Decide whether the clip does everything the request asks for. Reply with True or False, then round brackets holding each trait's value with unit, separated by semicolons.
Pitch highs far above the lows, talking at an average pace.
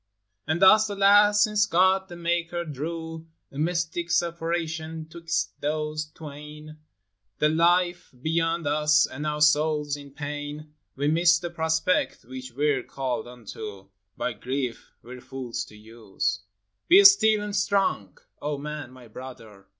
False (4.1 semitones; 145 wpm)